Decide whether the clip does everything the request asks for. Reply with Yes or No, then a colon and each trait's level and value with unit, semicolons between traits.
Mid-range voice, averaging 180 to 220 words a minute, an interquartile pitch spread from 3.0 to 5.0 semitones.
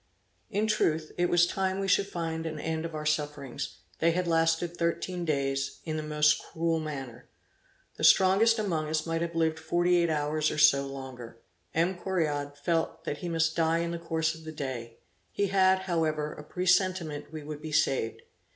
No: medium, 160 Hz; average, 190 wpm; narrow, 2.5 semitones